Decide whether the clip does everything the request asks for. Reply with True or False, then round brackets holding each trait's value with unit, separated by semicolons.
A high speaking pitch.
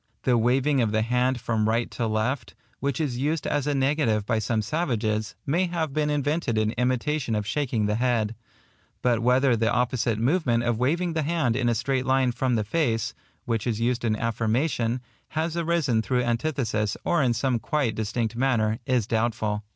False (120 Hz)